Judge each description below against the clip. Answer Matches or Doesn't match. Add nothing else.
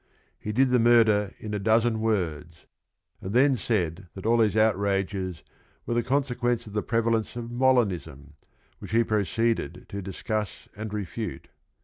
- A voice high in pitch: Doesn't match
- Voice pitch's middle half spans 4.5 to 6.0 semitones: Doesn't match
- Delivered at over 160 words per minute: Doesn't match